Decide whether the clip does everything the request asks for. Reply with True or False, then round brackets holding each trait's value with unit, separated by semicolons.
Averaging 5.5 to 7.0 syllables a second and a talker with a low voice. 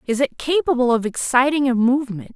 False (5.9 syllables/s; 260 Hz)